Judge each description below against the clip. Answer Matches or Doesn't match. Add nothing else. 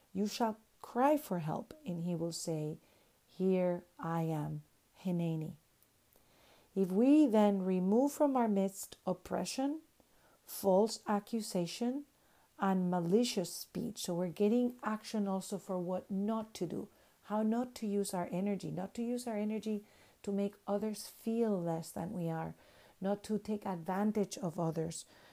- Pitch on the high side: Matches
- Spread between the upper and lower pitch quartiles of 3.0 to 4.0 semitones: Matches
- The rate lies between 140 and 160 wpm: Matches